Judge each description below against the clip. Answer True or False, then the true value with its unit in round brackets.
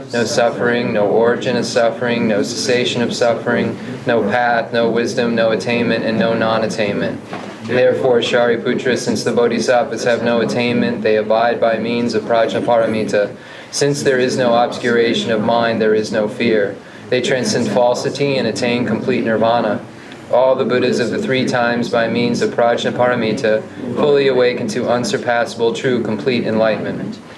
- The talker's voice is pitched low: True (120 Hz)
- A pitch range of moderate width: False (1.5 semitones)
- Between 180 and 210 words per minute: False (155 wpm)